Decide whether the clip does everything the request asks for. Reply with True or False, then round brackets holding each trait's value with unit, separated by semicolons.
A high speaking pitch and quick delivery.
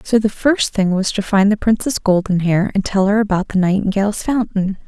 True (200 Hz; 210 wpm)